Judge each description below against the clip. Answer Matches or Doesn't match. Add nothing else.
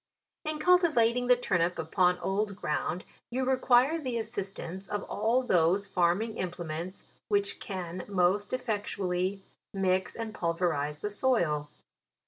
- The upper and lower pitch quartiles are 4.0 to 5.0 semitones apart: Matches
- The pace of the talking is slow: Matches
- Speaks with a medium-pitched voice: Doesn't match